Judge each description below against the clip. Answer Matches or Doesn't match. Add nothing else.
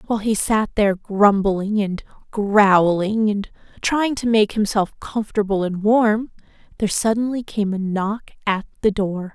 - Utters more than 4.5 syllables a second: Doesn't match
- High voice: Matches